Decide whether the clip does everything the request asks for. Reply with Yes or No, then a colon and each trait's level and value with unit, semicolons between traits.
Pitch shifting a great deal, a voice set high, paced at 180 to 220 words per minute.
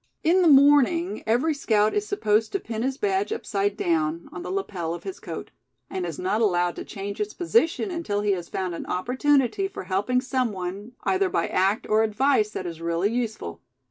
Yes: wide, 9.0 semitones; high, 225 Hz; average, 200 wpm